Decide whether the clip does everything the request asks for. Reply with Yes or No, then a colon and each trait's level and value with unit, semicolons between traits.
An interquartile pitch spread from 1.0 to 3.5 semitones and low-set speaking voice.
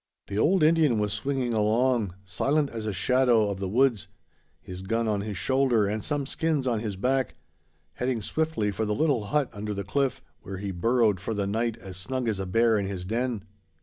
No: average, 4.4 semitones; low, 115 Hz